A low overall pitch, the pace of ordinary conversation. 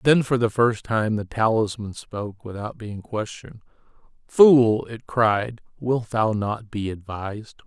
Yes: low, 110 Hz; average, 150 wpm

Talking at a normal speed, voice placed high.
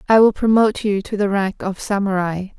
No: fast, 210 wpm; high, 200 Hz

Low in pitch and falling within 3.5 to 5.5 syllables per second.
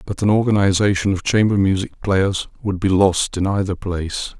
Yes: very low, 95 Hz; 5.1 syllables/s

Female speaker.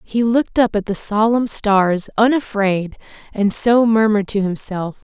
Yes: female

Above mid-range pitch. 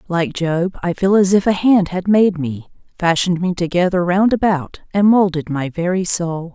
No: medium, 180 Hz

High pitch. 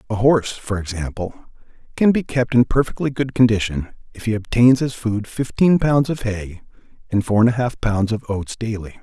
No: low, 115 Hz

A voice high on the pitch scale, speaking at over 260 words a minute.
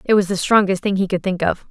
Yes: high, 195 Hz; fast, 315 wpm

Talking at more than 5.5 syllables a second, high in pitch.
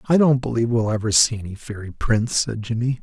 No: 6.1 syllables/s; low, 115 Hz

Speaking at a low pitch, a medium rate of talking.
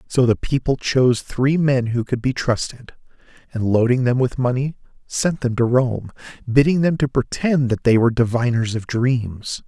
Yes: low, 125 Hz; average, 180 wpm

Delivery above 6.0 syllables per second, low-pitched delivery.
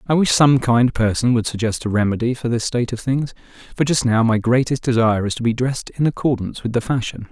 Yes: 6.3 syllables/s; low, 120 Hz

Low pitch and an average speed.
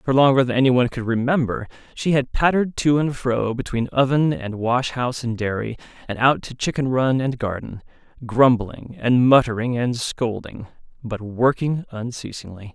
Yes: low, 125 Hz; average, 160 wpm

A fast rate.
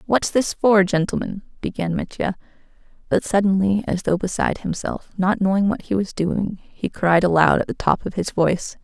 No: average, 185 wpm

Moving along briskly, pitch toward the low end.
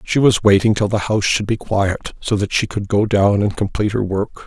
Yes: fast, 255 wpm; low, 105 Hz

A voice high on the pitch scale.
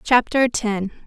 Yes: high, 230 Hz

